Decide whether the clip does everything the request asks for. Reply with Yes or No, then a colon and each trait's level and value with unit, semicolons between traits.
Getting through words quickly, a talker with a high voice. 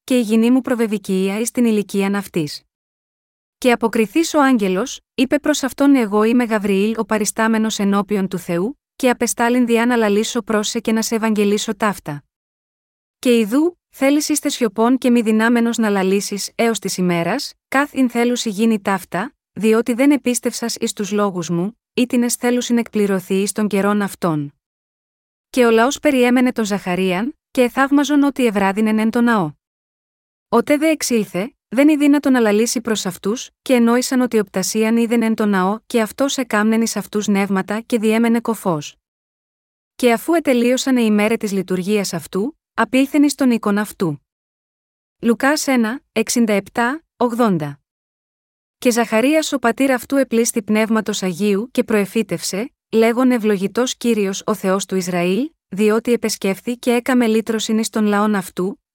No: average, 155 wpm; high, 225 Hz